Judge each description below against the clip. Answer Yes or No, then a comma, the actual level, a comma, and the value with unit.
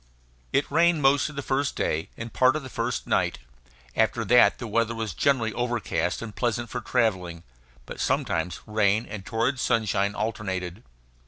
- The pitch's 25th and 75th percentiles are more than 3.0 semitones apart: Yes, average, 4.1 semitones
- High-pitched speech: No, low, 115 Hz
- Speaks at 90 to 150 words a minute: No, average, 165 wpm